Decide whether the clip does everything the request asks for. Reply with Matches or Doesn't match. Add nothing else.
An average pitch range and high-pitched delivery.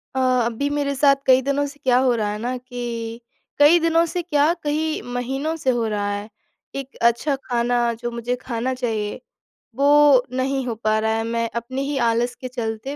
Matches